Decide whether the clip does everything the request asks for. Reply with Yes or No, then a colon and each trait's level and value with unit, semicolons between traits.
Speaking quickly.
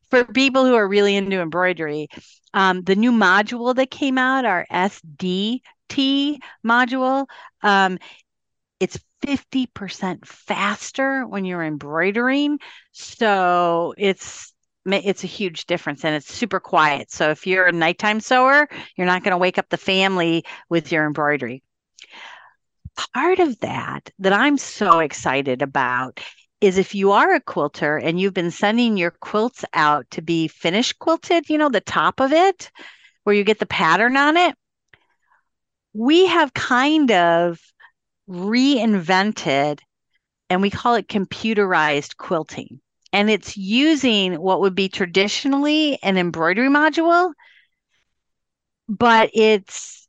No: slow, 135 wpm